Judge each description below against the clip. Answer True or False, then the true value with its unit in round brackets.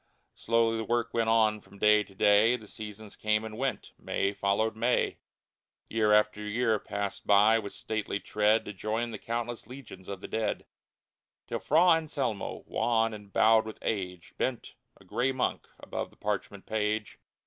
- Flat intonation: True (1.8 semitones)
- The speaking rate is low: False (170 wpm)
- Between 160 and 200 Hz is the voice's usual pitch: False (110 Hz)